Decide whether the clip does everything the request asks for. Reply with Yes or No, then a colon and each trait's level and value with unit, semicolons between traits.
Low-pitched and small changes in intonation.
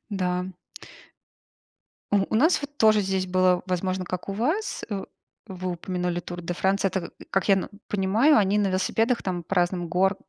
No: high, 190 Hz; narrow, 2.2 semitones